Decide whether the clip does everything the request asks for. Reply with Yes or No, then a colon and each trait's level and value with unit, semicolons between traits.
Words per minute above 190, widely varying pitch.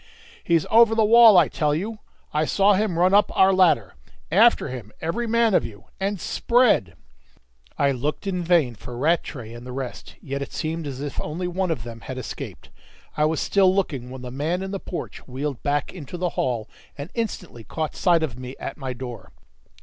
Yes: average, 200 wpm; wide, 6.7 semitones